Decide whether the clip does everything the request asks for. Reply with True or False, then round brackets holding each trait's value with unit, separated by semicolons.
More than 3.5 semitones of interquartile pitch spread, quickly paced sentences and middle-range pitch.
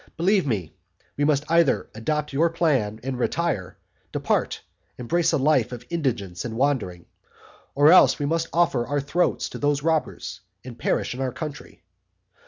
False (5.0 semitones; 160 wpm; 145 Hz)